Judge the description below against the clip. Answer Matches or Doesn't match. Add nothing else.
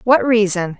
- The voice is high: Matches